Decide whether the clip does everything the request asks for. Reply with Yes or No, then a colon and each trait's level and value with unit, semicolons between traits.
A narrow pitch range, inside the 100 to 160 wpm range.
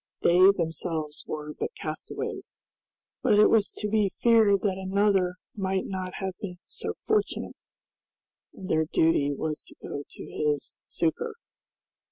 No: average, 4.3 semitones; average, 140 wpm